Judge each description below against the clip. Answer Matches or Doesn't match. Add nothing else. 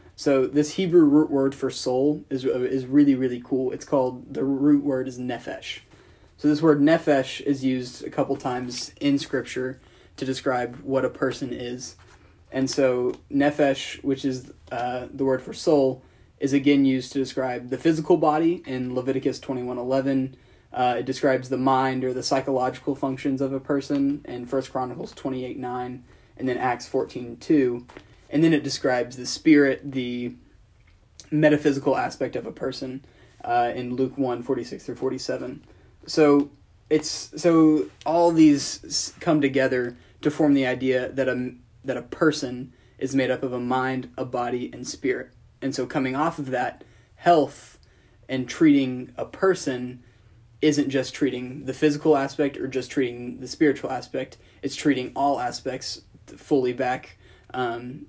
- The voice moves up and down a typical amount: Doesn't match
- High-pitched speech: Doesn't match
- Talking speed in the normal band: Matches